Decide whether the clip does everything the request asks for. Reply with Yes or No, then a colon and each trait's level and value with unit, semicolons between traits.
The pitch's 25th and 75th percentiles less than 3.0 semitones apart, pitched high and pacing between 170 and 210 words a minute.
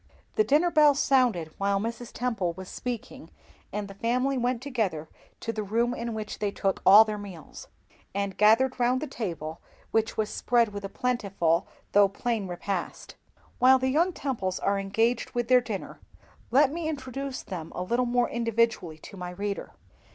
No: average, 4.2 semitones; high, 225 Hz; average, 175 wpm